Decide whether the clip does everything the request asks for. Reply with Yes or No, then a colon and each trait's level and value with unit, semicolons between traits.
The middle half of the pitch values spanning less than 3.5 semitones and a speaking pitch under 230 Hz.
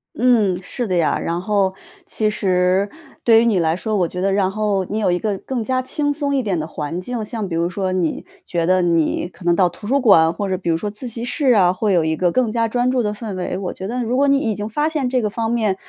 No: average, 4.6 semitones; high, 205 Hz